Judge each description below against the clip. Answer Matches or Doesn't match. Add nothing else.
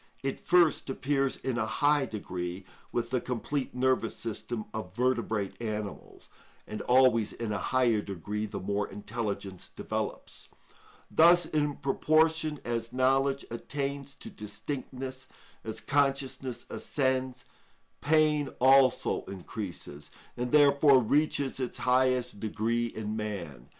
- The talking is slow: Matches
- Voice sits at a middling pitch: Doesn't match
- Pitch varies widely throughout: Doesn't match